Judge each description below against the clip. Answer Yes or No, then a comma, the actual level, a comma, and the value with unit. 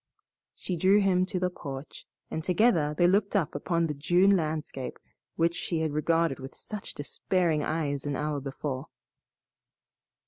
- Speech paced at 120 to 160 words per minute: Yes, average, 145 wpm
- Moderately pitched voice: Yes, medium, 165 Hz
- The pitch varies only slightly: No, average, 3.7 semitones